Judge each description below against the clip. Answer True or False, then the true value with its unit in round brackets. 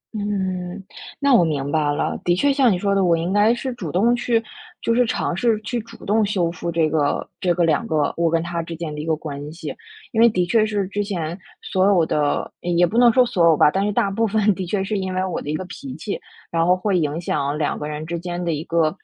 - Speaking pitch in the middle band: True (180 Hz)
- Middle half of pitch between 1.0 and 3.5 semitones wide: False (4.2 semitones)